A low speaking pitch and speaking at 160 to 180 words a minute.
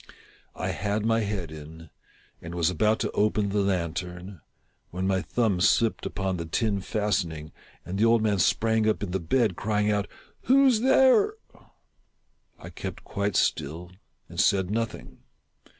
Yes: low, 100 Hz; average, 165 wpm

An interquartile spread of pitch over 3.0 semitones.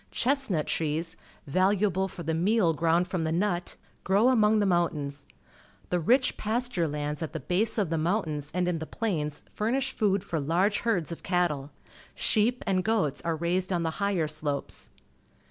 Yes: average, 4.6 semitones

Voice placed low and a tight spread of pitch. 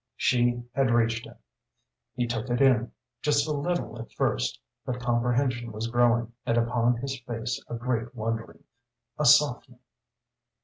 Yes: low, 120 Hz; narrow, 1.4 semitones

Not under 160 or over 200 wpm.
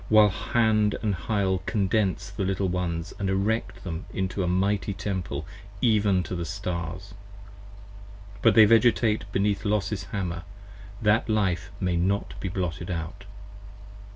No: average, 140 wpm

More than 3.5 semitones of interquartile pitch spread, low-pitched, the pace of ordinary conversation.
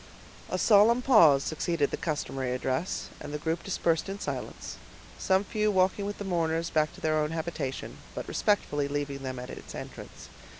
No: average, 5.0 semitones; medium, 160 Hz; average, 175 wpm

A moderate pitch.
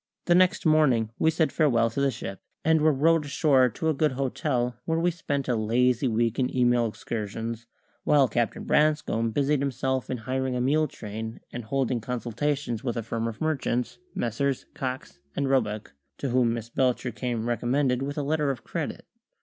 No: low, 130 Hz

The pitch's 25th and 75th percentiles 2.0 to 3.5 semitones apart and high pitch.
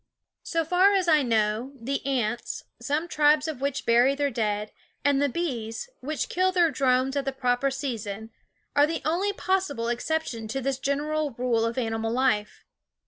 No: average, 4.7 semitones; very high, 270 Hz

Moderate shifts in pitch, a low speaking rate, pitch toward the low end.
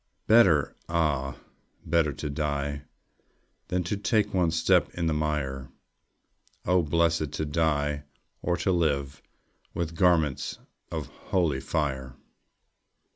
Yes: average, 3.0 semitones; slow, 115 wpm; very low, 80 Hz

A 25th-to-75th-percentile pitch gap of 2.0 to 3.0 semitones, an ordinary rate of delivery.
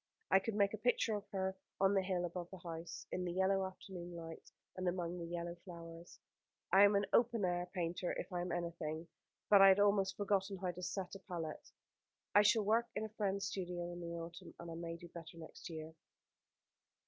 No: narrow, 2.5 semitones; fast, 210 wpm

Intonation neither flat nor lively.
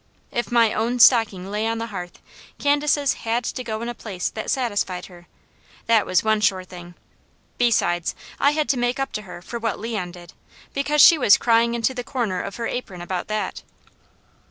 Yes: average, 4.3 semitones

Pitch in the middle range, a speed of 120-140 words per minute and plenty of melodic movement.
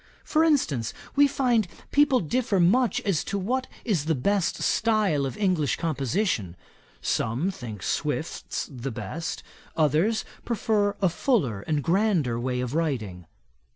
Yes: medium, 170 Hz; slow, 135 wpm; wide, 8.4 semitones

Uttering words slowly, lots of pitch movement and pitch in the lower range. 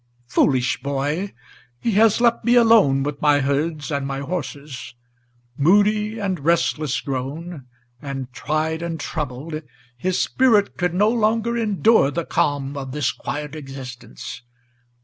No: slow, 130 wpm; wide, 6.5 semitones; medium, 150 Hz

